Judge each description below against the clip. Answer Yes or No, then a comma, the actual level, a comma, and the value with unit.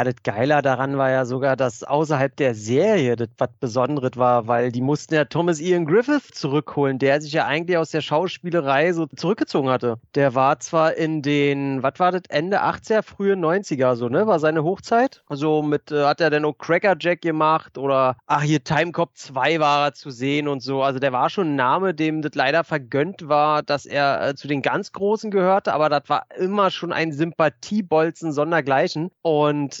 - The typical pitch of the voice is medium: Yes, medium, 150 Hz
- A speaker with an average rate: No, fast, 200 wpm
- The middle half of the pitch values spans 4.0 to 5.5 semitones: No, average, 3.3 semitones